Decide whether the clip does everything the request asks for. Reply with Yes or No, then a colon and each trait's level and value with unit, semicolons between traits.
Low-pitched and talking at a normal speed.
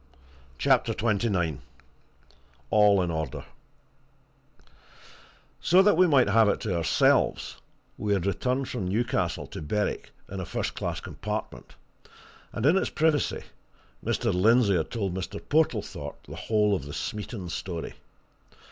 No: low, 105 Hz; slow, 130 wpm